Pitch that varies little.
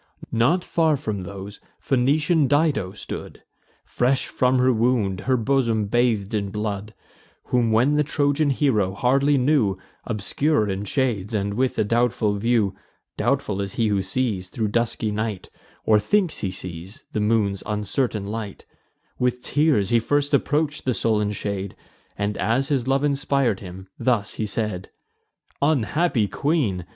No: average, 5.0 semitones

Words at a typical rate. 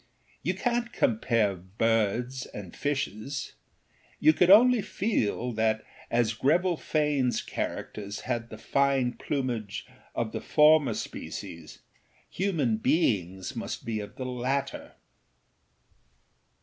No: slow, 110 wpm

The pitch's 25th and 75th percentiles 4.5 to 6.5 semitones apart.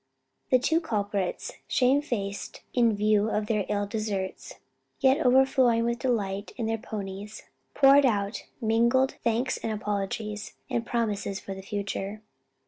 No: average, 3.2 semitones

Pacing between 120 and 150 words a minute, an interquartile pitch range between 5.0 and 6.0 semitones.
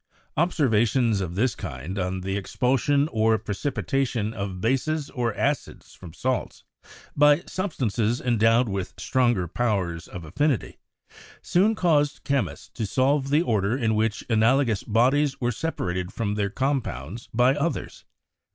Yes: slow, 135 wpm; wide, 5.4 semitones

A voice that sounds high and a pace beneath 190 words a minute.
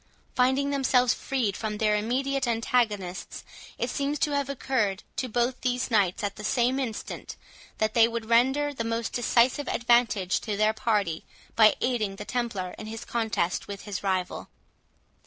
Yes: high, 230 Hz; average, 160 wpm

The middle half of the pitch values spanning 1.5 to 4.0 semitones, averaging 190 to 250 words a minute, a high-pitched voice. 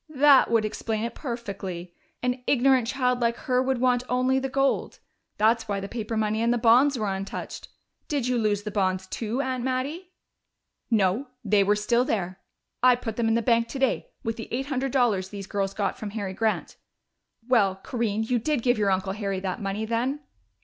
Yes: average, 3.6 semitones; average, 195 wpm; high, 230 Hz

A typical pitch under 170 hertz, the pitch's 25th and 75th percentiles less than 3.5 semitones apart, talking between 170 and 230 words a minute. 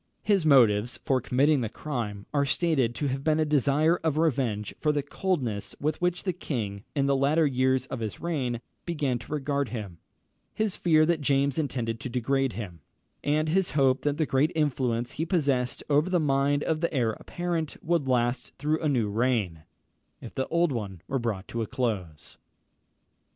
No: low, 135 Hz; average, 4.5 semitones; average, 185 wpm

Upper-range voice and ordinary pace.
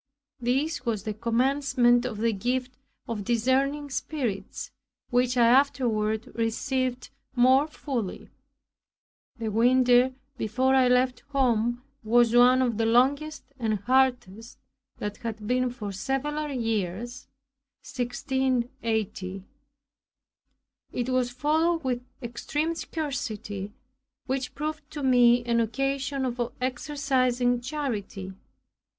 No: high, 245 Hz; slow, 105 wpm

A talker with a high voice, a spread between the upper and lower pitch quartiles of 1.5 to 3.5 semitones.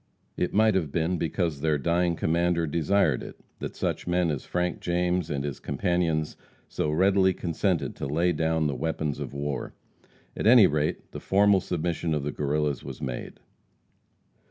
No: very low, 85 Hz; average, 3.1 semitones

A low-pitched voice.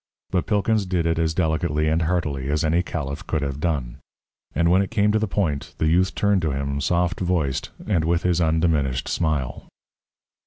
Yes: very low, 80 Hz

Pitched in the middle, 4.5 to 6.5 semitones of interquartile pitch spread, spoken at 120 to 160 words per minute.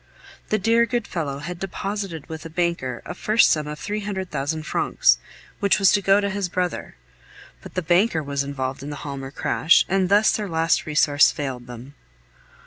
No: medium, 170 Hz; wide, 5.4 semitones; average, 190 wpm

